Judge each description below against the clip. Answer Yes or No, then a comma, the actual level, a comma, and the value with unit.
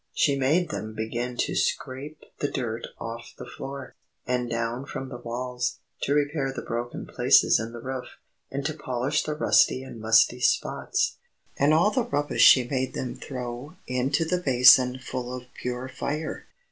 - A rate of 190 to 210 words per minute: No, average, 170 wpm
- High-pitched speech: No, low, 130 Hz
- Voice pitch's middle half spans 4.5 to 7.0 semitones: No, narrow, 2.6 semitones